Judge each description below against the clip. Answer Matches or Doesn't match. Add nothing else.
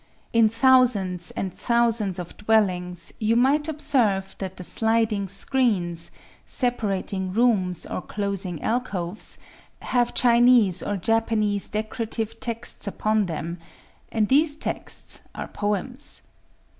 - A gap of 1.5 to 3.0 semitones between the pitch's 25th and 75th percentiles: Doesn't match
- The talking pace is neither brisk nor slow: Doesn't match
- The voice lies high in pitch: Matches